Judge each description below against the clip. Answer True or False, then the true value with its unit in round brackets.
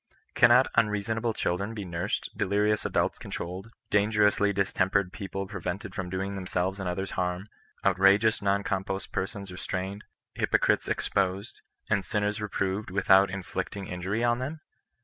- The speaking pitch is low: True (100 Hz)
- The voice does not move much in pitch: True (1.8 semitones)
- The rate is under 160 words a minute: True (140 wpm)